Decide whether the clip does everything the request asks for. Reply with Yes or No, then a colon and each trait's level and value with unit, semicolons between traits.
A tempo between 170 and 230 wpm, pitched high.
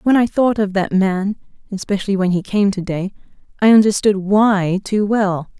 No: average, 150 wpm; high, 200 Hz